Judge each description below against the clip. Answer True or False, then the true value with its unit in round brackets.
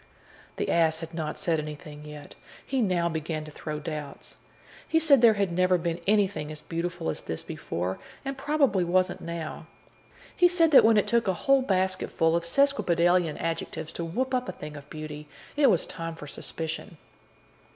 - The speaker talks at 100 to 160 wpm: False (185 wpm)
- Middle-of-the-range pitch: True (170 Hz)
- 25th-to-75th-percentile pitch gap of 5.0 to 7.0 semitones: True (5.4 semitones)